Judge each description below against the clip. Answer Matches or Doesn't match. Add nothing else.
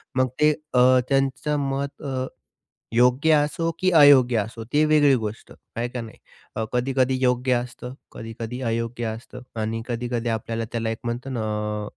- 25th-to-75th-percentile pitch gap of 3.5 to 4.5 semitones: Doesn't match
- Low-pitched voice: Matches